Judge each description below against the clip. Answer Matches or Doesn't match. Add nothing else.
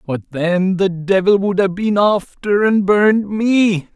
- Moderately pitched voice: Doesn't match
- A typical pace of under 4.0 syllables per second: Matches